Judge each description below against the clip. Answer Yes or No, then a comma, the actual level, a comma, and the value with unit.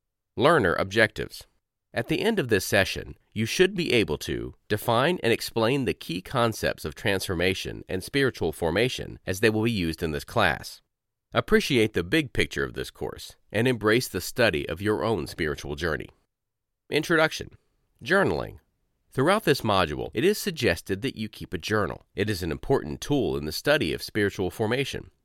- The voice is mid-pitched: No, low, 110 Hz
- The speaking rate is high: No, average, 170 wpm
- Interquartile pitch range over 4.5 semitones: Yes, average, 5.1 semitones